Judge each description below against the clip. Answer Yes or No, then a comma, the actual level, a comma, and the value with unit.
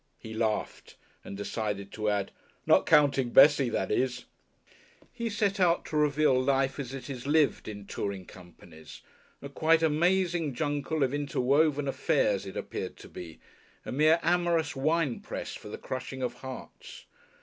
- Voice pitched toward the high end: No, medium, 140 Hz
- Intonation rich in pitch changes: No, average, 4.7 semitones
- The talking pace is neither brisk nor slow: Yes, average, 150 wpm